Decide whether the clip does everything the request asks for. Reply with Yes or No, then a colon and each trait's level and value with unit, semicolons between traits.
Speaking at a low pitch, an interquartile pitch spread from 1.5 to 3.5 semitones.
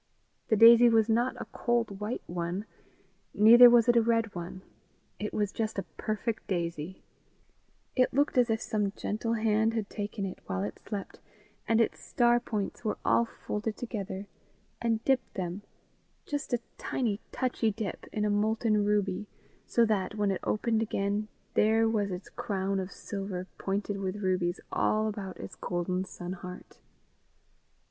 No: high, 210 Hz; average, 2.8 semitones